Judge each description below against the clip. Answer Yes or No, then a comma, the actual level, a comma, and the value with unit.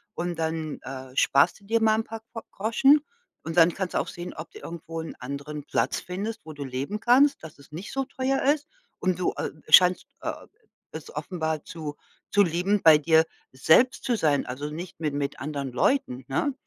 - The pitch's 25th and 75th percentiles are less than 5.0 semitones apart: No, wide, 6.5 semitones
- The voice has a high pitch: No, medium, 165 Hz